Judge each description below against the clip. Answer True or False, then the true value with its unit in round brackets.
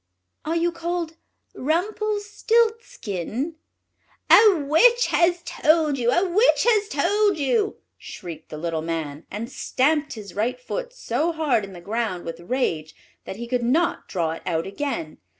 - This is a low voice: False (290 Hz)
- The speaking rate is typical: True (150 wpm)